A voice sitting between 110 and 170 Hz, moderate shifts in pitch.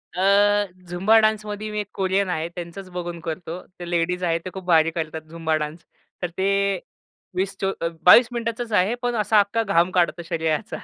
No: medium, 185 Hz; average, 3.5 semitones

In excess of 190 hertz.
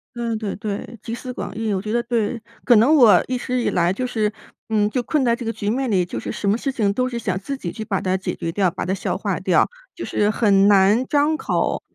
Yes: high, 220 Hz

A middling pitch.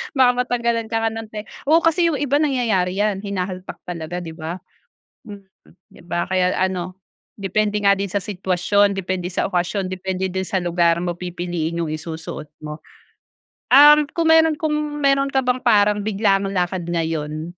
No: high, 195 Hz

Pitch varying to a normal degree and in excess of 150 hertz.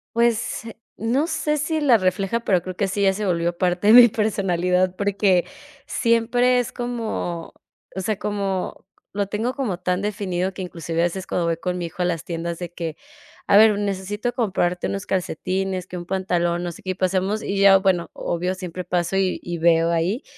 Yes: average, 3.1 semitones; high, 190 Hz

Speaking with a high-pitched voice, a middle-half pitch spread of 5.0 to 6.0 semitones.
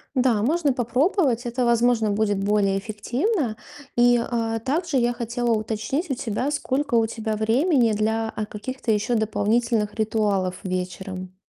No: high, 225 Hz; average, 2.9 semitones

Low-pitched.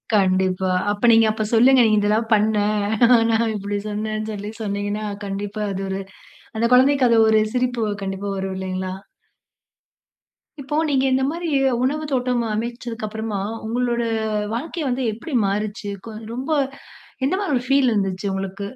No: high, 220 Hz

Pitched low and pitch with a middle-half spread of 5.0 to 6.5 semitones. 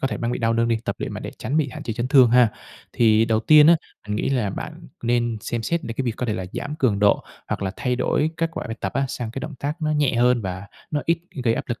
No: low, 120 Hz; average, 4.0 semitones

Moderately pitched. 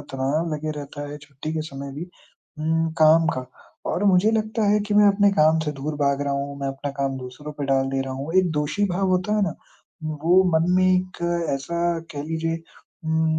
Yes: medium, 155 Hz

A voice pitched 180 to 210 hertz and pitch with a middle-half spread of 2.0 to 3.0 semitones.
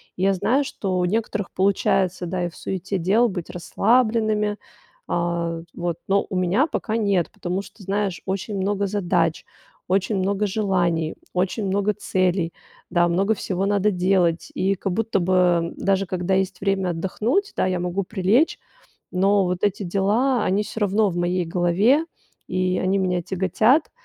Yes: high, 190 Hz; narrow, 2.4 semitones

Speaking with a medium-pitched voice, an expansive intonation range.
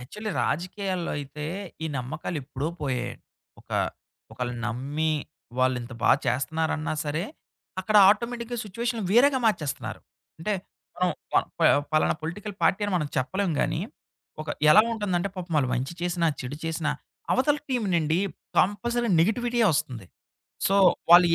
Yes: medium, 170 Hz; wide, 6.6 semitones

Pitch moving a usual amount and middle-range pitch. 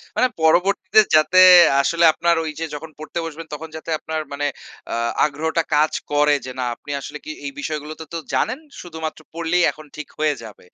No: narrow, 2.0 semitones; medium, 160 Hz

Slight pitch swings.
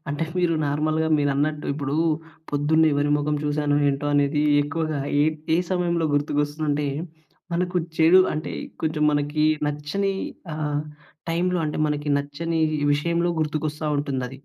Yes: narrow, 1.8 semitones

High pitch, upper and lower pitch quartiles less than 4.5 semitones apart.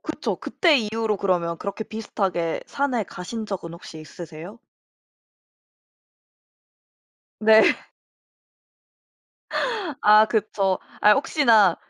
Yes: high, 210 Hz; average, 3.8 semitones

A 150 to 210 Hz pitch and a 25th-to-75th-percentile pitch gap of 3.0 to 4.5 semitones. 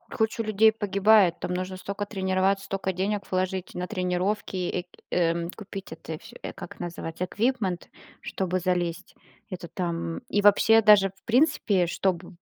No: high, 190 Hz; narrow, 2.5 semitones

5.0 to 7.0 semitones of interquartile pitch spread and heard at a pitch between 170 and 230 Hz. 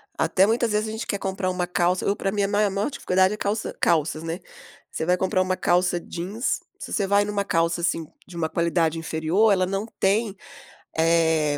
No: average, 3.2 semitones; medium, 185 Hz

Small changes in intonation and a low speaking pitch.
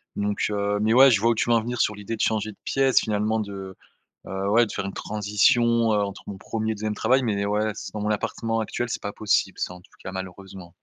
Yes: narrow, 2.0 semitones; low, 105 Hz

